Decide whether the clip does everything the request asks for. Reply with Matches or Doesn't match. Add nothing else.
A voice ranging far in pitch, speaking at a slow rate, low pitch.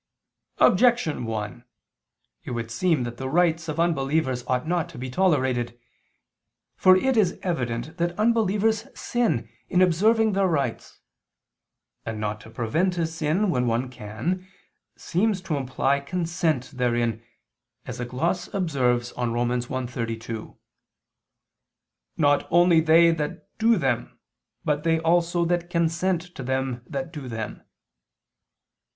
Doesn't match